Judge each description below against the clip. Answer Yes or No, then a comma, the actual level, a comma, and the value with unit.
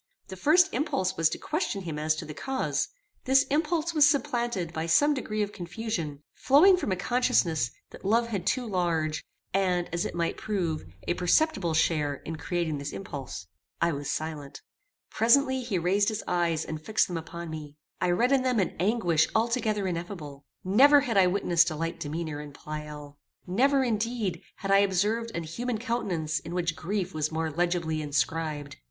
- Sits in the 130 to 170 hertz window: No, medium, 180 Hz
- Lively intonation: Yes, wide, 6.4 semitones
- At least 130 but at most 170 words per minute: No, average, 180 wpm